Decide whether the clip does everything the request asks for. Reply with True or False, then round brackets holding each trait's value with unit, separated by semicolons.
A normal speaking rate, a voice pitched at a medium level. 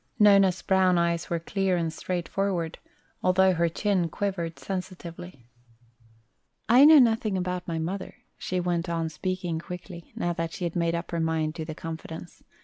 True (160 wpm; 175 Hz)